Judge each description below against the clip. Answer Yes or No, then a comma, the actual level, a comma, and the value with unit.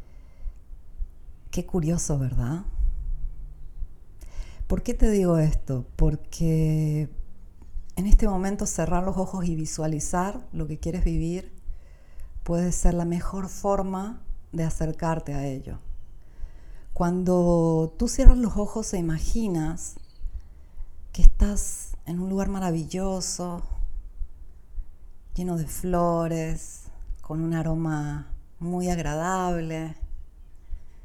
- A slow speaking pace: Yes, slow, 100 wpm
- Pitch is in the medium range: Yes, medium, 155 Hz